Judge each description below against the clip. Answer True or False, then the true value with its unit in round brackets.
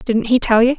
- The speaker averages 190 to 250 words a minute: False (305 wpm)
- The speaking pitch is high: True (235 Hz)